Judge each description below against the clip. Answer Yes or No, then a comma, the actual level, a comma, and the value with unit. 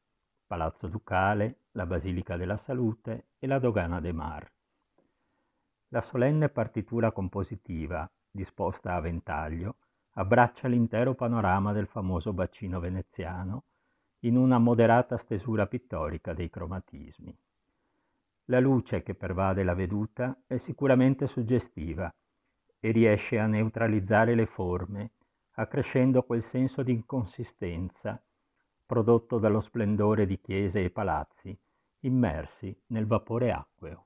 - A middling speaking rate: No, slow, 110 wpm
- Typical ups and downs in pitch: Yes, average, 4.5 semitones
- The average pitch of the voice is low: Yes, low, 110 Hz